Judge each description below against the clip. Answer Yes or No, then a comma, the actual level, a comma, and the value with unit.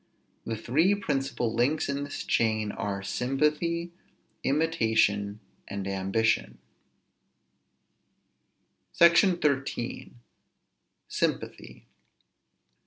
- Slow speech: Yes, slow, 70 wpm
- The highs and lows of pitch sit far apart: Yes, wide, 6.2 semitones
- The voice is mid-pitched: No, low, 130 Hz